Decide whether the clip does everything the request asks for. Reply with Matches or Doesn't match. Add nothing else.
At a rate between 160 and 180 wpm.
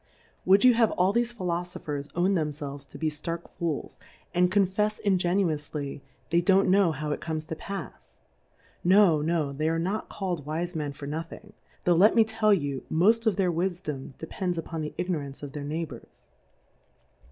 Matches